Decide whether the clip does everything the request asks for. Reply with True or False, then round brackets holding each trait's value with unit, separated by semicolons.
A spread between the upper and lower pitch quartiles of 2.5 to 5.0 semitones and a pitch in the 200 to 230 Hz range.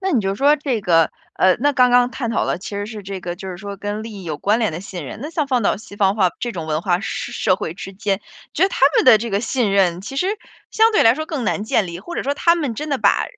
False (5.4 semitones; 210 Hz)